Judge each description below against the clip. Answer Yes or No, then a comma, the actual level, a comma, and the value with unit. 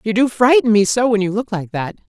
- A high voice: Yes, high, 215 Hz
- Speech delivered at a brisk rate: Yes, fast, 280 wpm